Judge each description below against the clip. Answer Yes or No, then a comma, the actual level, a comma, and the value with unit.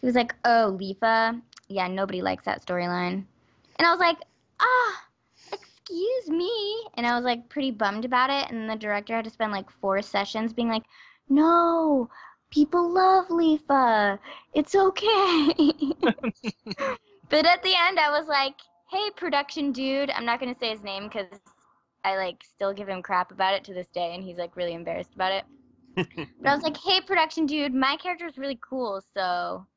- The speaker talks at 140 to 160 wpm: No, average, 185 wpm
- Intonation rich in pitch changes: Yes, wide, 8.0 semitones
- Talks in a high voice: Yes, very high, 250 Hz